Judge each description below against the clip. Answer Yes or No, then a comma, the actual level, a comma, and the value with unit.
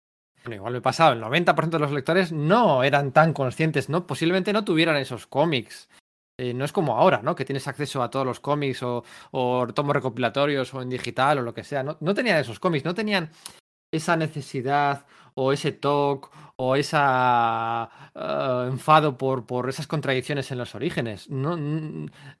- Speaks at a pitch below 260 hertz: Yes, medium, 140 Hz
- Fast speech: No, average, 180 wpm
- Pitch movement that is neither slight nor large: Yes, average, 3.9 semitones